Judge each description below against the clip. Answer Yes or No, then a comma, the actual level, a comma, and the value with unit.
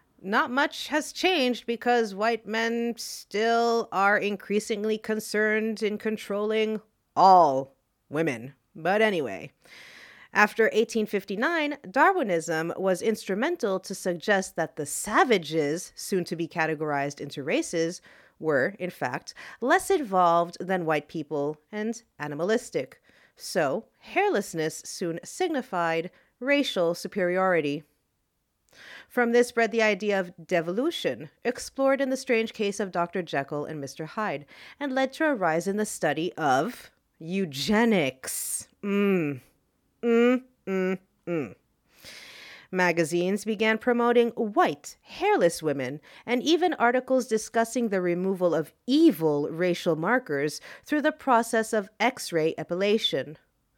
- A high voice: Yes, high, 205 Hz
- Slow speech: Yes, slow, 115 wpm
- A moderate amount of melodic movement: No, wide, 5.8 semitones